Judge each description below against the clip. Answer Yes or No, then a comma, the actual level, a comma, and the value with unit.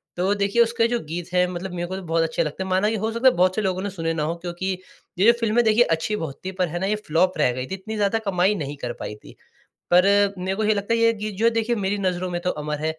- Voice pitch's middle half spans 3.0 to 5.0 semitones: Yes, average, 3.7 semitones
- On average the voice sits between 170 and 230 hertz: Yes, high, 190 Hz